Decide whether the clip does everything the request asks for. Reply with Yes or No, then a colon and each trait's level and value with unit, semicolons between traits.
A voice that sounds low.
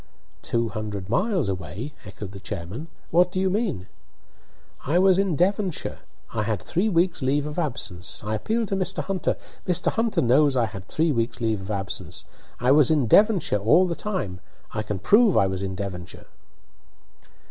Yes: low, 130 Hz